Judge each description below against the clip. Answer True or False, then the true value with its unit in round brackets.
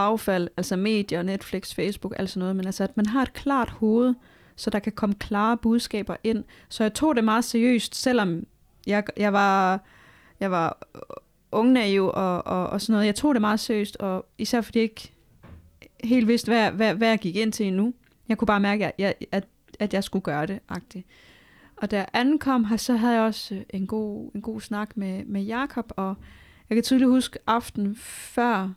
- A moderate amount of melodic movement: True (3.0 semitones)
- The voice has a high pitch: True (215 Hz)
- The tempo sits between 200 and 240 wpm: True (205 wpm)